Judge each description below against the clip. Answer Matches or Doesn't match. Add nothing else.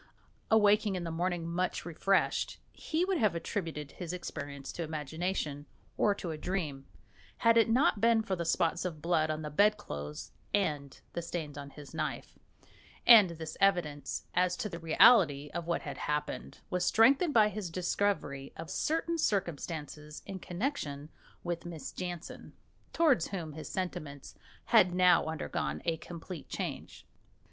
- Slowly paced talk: Doesn't match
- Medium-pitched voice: Matches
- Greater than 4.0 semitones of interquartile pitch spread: Matches